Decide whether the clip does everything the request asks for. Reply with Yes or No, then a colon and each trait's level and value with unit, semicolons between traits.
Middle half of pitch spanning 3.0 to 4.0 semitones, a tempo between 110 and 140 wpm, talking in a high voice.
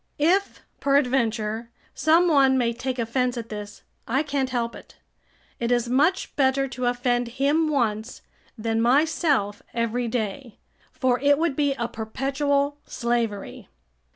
Yes: average, 3.3 semitones; slow, 135 wpm; very high, 250 Hz